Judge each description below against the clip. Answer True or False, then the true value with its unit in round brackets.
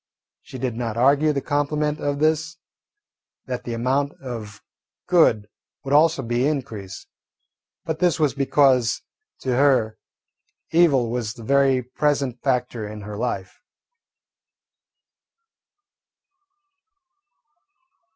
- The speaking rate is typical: False (105 wpm)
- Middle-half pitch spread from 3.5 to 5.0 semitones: True (3.8 semitones)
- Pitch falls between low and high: False (130 Hz)